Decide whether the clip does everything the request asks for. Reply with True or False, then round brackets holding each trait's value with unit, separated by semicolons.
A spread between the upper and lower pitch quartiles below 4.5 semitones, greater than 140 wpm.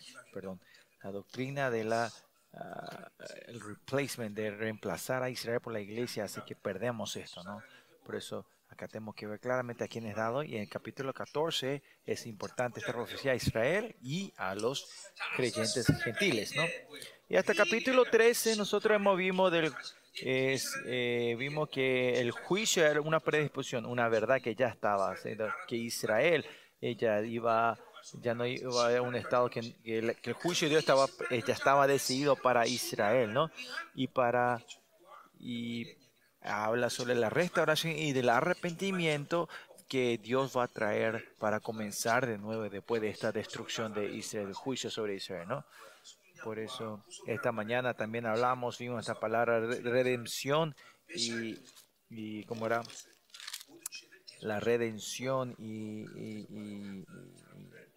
True (3.4 semitones; 150 wpm)